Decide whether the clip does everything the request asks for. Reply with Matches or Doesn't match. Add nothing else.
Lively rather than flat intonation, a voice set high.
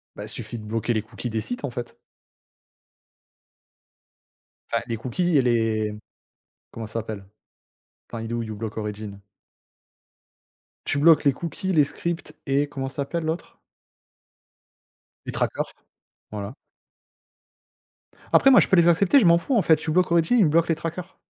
Doesn't match